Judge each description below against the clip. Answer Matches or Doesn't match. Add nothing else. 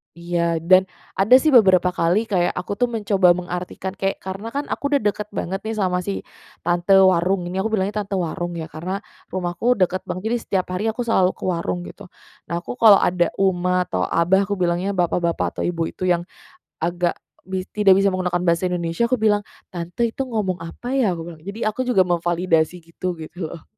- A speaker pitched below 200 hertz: Matches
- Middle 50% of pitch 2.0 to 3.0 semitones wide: Matches